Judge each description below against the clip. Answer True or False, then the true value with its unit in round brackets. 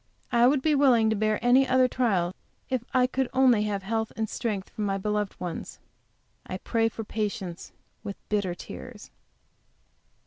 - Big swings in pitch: False (3.5 semitones)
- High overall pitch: True (220 Hz)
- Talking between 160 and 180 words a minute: True (165 wpm)